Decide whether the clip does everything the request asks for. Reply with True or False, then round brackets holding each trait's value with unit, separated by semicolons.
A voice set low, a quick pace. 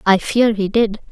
False (210 Hz; 215 wpm)